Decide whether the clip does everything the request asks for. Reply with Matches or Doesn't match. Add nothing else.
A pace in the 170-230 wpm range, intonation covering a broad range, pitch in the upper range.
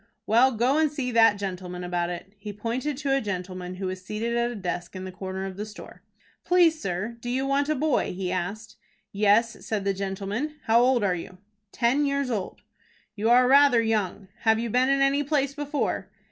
Matches